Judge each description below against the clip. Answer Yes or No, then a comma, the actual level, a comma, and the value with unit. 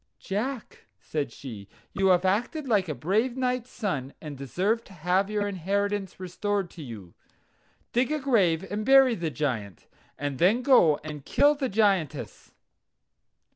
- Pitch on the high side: Yes, high, 195 Hz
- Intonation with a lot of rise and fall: Yes, wide, 6.8 semitones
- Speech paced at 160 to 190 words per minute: No, average, 150 wpm